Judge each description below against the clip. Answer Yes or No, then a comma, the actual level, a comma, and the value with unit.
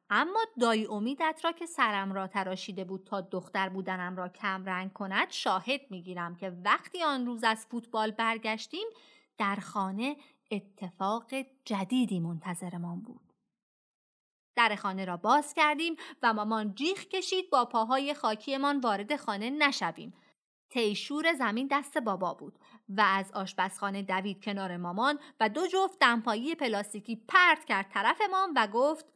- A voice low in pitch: No, high, 225 Hz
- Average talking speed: Yes, average, 140 wpm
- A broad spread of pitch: Yes, wide, 6.6 semitones